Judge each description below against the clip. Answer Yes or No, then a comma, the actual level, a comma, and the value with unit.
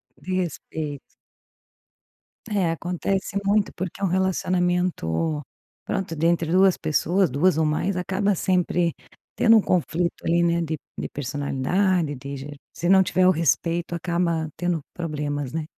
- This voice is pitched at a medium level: Yes, medium, 170 Hz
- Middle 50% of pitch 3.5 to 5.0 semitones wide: No, average, 3.1 semitones